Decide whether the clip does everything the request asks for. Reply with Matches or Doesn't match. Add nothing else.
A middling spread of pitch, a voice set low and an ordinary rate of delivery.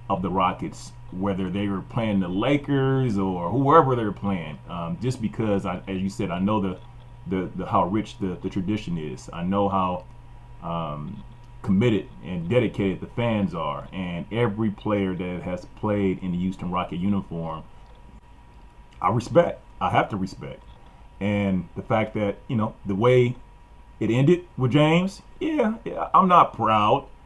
Matches